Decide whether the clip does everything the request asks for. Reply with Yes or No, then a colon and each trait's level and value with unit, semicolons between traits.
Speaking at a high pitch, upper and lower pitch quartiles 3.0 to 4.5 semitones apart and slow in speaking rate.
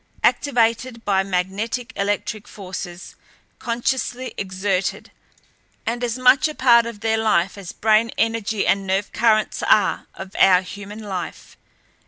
Yes: high, 215 Hz; average, 3.3 semitones; slow, 130 wpm